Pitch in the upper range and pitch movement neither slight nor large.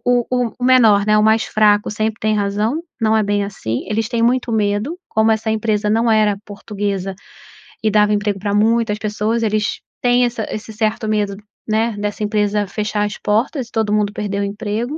No: high, 215 Hz; narrow, 1.4 semitones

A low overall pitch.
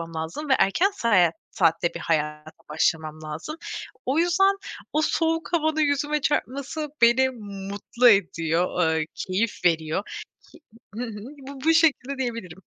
No: high, 235 Hz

